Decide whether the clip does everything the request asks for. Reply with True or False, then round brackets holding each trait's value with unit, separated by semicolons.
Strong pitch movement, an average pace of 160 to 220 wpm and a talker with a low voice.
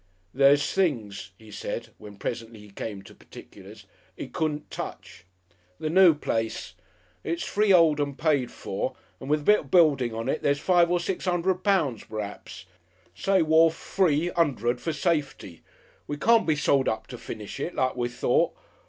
False (6.2 semitones; 170 wpm; 145 Hz)